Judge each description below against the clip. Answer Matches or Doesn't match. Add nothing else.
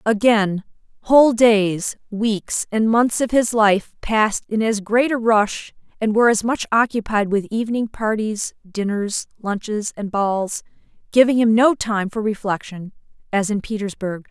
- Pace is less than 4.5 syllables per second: Matches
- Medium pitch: Doesn't match